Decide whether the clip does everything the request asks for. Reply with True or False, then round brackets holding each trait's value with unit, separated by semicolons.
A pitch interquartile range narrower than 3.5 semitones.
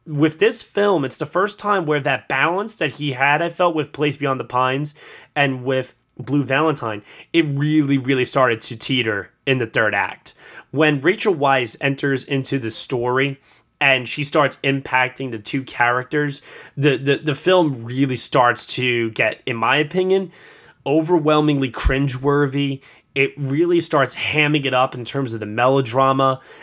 True (2.8 semitones)